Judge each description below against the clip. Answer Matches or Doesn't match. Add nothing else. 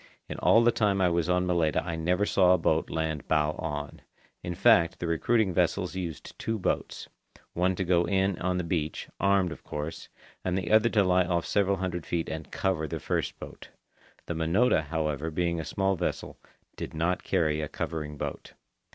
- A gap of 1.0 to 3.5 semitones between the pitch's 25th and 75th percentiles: Matches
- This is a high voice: Doesn't match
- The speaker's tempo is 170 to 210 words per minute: Matches